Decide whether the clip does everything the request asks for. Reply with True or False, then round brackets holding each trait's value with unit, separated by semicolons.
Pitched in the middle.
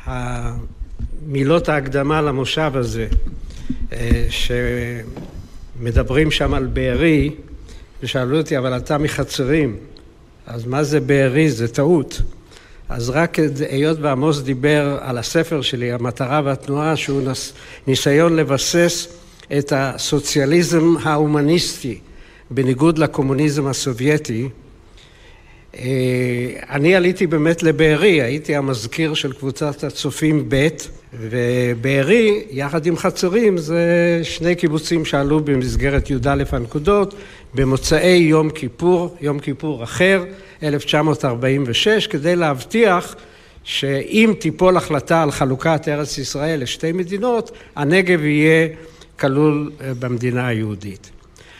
True (145 Hz)